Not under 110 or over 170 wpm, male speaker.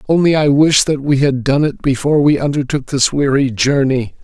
No: average, 200 wpm; male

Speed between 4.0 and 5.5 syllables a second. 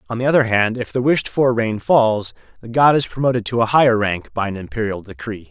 No: 5.8 syllables/s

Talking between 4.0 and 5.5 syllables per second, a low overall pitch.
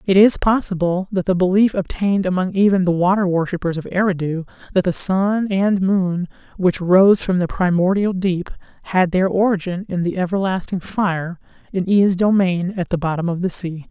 No: 5.0 syllables/s; medium, 185 Hz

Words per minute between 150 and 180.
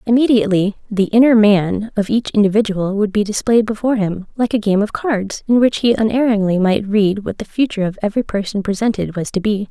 No: fast, 205 wpm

